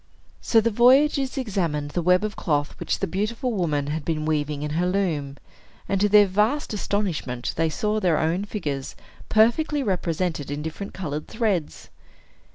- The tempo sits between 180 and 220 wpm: No, average, 165 wpm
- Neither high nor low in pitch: Yes, medium, 180 Hz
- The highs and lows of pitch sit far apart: Yes, wide, 5.7 semitones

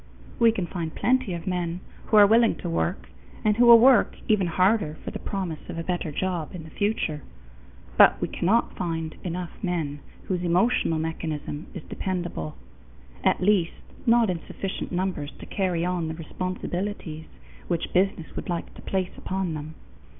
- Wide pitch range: No, average, 3.3 semitones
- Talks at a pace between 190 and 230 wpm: No, average, 170 wpm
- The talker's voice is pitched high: No, medium, 180 Hz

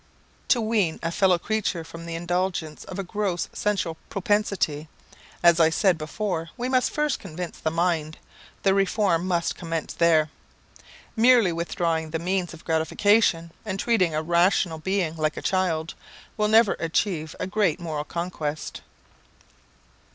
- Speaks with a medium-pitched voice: Yes, medium, 175 Hz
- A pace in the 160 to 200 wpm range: No, average, 145 wpm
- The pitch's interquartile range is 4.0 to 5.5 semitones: No, average, 3.5 semitones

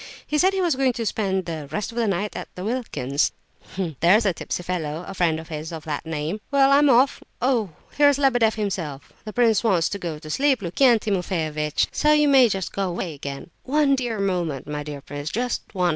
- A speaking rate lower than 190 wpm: No, fast, 205 wpm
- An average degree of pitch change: No, wide, 7.3 semitones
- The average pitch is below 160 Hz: No, high, 195 Hz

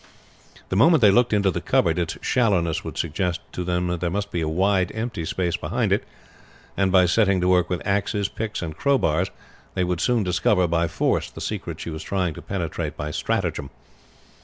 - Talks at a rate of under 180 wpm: No, average, 200 wpm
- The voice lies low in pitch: Yes, very low, 90 Hz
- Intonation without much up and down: No, average, 3.0 semitones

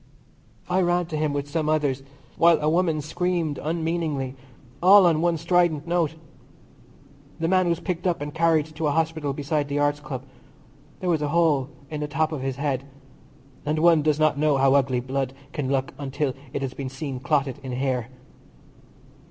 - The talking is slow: No, average, 185 wpm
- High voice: No, medium, 150 Hz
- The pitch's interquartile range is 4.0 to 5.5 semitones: No, average, 3.1 semitones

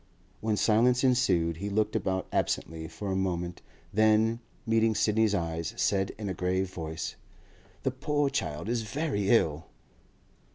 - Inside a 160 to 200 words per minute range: No, average, 140 wpm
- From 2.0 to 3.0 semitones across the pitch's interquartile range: No, average, 4.3 semitones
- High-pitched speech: No, low, 105 Hz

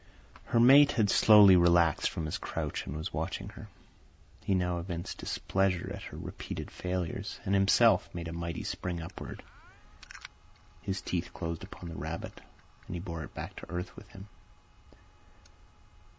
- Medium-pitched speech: No, very low, 90 Hz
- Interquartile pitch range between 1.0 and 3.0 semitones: Yes, narrow, 2.5 semitones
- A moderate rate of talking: Yes, average, 155 wpm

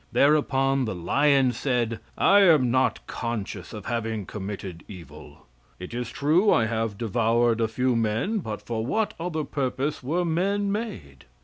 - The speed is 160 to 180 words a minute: No, average, 150 wpm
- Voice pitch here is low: Yes, low, 120 Hz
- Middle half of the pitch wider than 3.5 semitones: Yes, average, 5.3 semitones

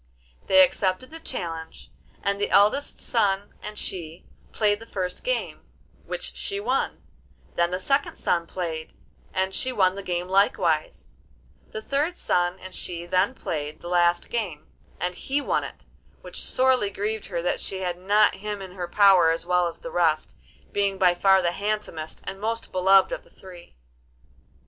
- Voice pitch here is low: No, high, 190 Hz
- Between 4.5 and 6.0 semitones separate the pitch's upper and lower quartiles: No, average, 3.2 semitones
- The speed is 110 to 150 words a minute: No, average, 170 wpm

